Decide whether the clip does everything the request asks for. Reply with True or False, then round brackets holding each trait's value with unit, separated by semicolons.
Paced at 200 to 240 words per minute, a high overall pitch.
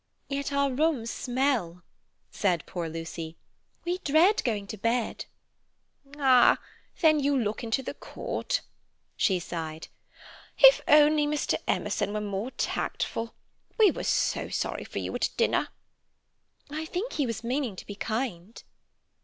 False (135 wpm; 245 Hz)